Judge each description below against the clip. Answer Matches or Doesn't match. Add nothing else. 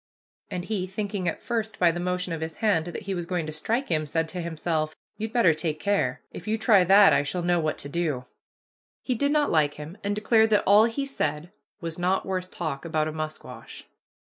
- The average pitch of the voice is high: Doesn't match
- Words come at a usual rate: Doesn't match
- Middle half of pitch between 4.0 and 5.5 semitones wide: Matches